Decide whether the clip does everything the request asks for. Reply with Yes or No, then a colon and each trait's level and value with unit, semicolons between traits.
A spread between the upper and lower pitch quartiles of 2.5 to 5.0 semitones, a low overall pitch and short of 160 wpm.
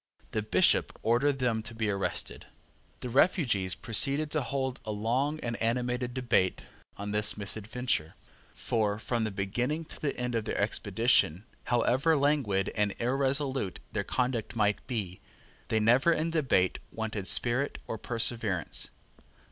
Yes: average, 4.0 semitones; low, 115 Hz; average, 140 wpm